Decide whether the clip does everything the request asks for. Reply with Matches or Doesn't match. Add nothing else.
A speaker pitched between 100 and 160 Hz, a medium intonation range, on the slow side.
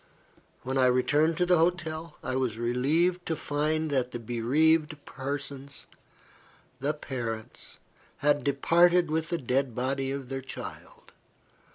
Matches